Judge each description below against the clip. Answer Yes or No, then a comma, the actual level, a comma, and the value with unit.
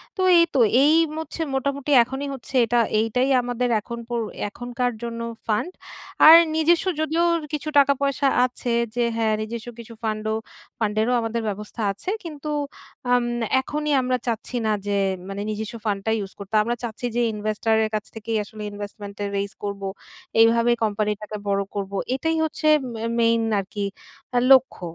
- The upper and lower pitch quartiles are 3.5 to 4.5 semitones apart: Yes, average, 3.9 semitones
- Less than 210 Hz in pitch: No, high, 230 Hz